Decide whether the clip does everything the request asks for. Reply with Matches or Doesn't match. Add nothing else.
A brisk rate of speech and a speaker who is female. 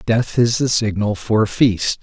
Doesn't match